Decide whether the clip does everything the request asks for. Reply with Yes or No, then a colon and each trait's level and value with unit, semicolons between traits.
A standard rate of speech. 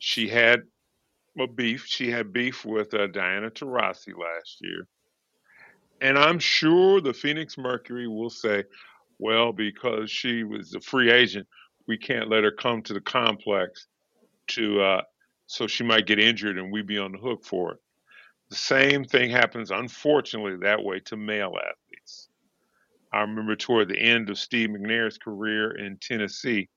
Yes: average, 160 wpm